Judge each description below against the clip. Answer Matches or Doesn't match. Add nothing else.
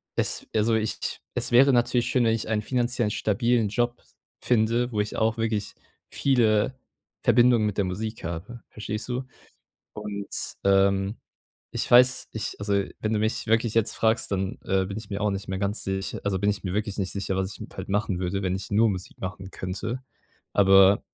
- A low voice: Matches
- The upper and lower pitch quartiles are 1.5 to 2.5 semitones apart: Doesn't match